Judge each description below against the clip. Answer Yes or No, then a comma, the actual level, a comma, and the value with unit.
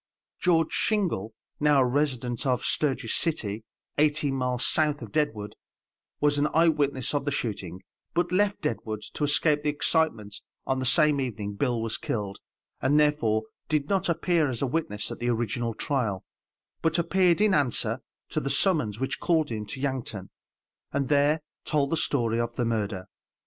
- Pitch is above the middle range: No, medium, 140 Hz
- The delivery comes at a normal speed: Yes, average, 170 wpm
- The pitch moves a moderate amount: Yes, average, 5.0 semitones